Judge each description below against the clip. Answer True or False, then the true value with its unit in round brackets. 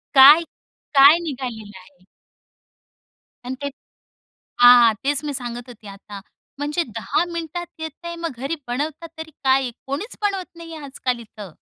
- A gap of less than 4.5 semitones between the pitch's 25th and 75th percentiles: False (4.8 semitones)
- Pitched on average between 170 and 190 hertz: False (275 Hz)